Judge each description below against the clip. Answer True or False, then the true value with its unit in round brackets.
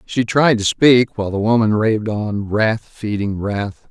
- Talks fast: False (185 wpm)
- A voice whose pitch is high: False (110 Hz)